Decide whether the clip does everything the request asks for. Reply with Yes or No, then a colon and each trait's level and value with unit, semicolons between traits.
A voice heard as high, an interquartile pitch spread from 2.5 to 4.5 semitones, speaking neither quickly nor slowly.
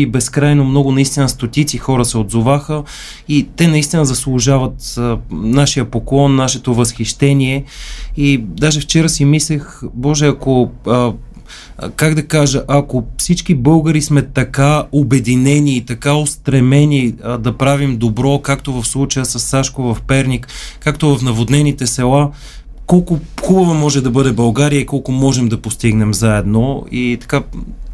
No: low, 135 Hz; average, 2.9 semitones; average, 140 wpm